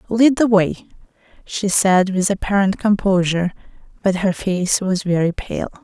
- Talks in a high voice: Yes, high, 195 Hz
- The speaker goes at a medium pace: Yes, average, 145 wpm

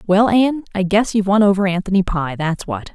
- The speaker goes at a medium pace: No, fast, 225 wpm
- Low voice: No, high, 195 Hz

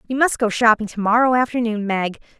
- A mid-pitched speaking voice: No, high, 230 Hz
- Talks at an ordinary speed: Yes, average, 175 wpm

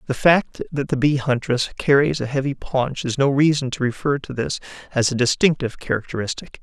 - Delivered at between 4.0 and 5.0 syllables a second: No, 5.6 syllables/s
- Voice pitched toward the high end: No, low, 135 Hz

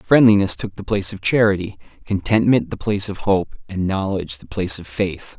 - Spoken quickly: No, average, 190 wpm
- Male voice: Yes, male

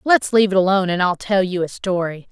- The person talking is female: Yes, female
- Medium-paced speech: No, fast, 260 wpm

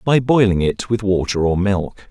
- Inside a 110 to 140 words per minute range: No, average, 200 wpm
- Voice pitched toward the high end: No, low, 100 Hz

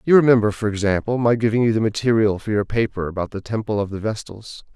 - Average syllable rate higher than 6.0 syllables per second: Yes, 6.4 syllables/s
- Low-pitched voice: Yes, low, 110 Hz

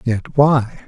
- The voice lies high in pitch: No, low, 125 Hz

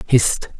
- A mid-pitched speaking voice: No, low, 115 Hz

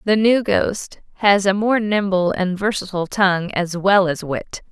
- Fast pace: No, average, 180 wpm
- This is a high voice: Yes, high, 195 Hz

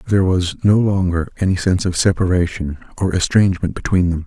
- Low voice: Yes, very low, 90 Hz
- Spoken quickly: No, average, 170 wpm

